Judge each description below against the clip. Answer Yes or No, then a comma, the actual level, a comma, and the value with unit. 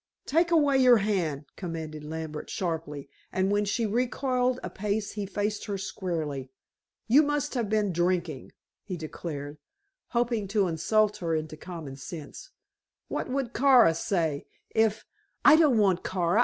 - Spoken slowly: No, average, 150 wpm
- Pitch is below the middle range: No, high, 195 Hz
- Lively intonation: Yes, wide, 6.5 semitones